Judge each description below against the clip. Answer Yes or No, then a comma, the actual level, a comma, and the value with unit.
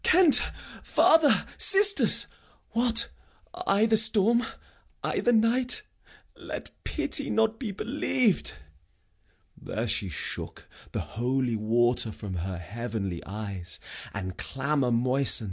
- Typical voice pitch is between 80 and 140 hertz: Yes, low, 135 Hz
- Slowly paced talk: Yes, slow, 110 wpm